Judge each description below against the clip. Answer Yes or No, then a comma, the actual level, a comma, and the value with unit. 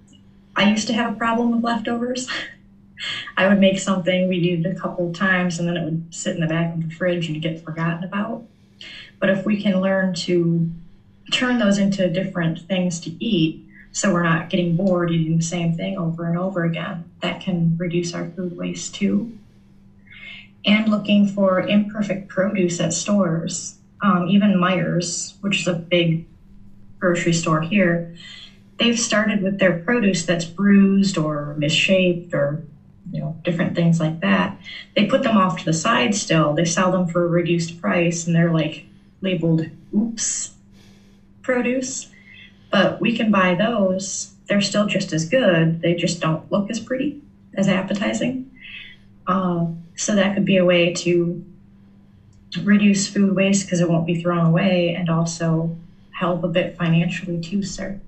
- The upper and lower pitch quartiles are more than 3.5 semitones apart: No, average, 2.8 semitones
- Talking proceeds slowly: No, average, 170 wpm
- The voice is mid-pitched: Yes, medium, 180 Hz